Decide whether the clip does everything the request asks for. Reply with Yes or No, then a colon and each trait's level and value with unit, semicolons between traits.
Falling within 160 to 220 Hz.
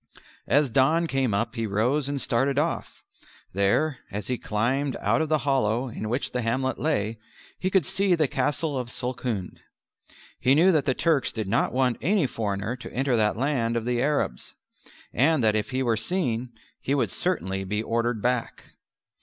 No: low, 125 Hz